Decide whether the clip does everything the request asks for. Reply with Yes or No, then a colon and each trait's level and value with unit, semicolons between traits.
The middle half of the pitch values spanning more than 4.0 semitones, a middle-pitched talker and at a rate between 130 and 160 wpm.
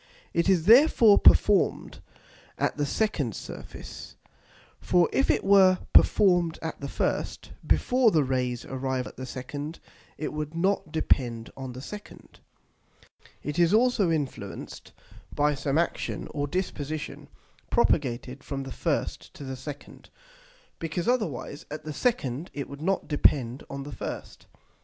Yes: wide, 5.4 semitones; medium, 150 Hz; average, 140 wpm